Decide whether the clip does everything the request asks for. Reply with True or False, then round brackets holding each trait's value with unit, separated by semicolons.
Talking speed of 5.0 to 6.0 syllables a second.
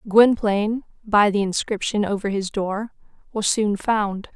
False (4.2 syllables/s)